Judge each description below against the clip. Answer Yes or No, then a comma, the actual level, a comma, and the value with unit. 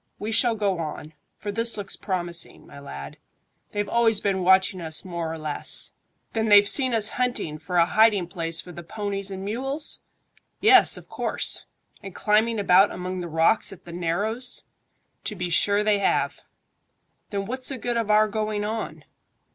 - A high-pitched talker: Yes, high, 200 Hz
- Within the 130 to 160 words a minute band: No, average, 175 wpm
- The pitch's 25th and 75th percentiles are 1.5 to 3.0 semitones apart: No, average, 4.0 semitones